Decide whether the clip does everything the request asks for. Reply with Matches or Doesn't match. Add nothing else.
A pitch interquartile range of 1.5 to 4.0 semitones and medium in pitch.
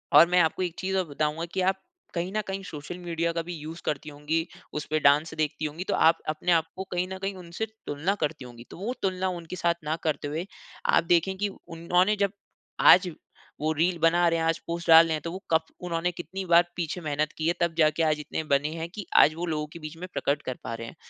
Matches